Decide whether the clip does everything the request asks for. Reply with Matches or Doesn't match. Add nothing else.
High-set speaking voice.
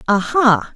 Matches